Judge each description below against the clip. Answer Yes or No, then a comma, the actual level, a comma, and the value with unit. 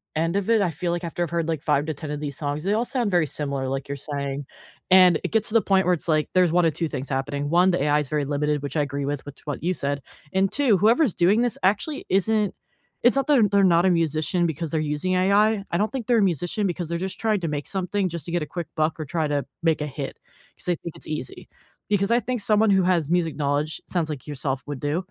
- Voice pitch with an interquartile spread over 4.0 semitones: Yes, average, 4.7 semitones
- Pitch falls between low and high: Yes, medium, 170 Hz